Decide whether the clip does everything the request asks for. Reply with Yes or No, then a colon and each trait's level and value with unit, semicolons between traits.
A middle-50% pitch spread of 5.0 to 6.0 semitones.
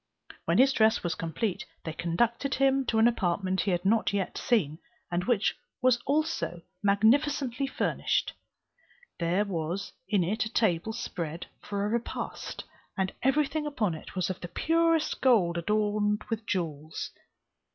Yes: wide, 5.4 semitones